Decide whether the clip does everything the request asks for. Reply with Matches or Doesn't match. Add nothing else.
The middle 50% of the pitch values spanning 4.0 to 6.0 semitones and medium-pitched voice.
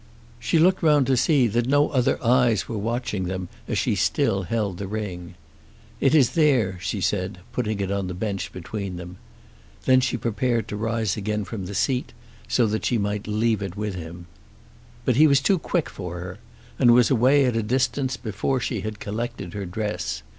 Doesn't match